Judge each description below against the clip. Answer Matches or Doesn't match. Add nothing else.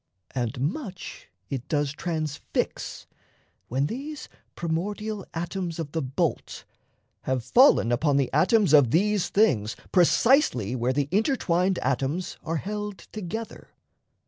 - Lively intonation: Matches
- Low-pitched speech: Doesn't match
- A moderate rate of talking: Doesn't match